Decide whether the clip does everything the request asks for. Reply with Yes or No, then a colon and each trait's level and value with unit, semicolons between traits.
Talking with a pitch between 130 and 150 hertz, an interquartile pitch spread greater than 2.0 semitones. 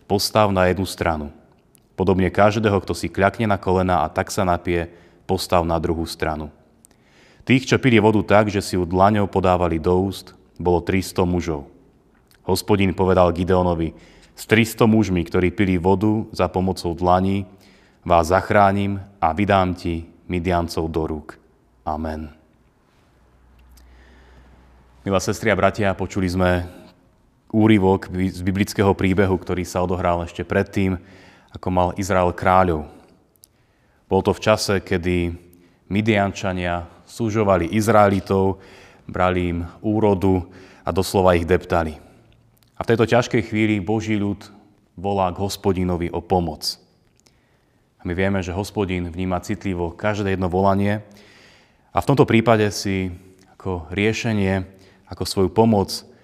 No: very low, 95 Hz; narrow, 2.5 semitones